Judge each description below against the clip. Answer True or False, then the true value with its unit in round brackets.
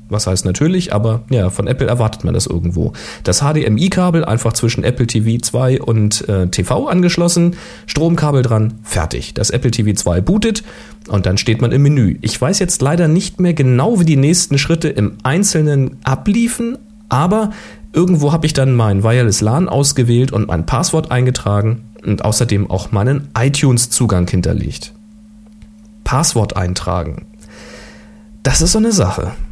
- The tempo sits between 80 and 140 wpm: False (150 wpm)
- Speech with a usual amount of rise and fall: False (7.0 semitones)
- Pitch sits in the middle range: False (125 Hz)